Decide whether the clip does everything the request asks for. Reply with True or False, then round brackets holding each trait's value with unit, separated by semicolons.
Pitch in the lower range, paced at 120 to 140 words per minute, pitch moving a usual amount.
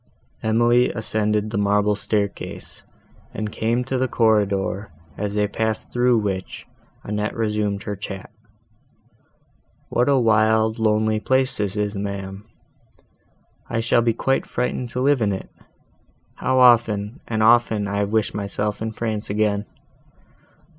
False (110 Hz; 135 wpm; 2.0 semitones)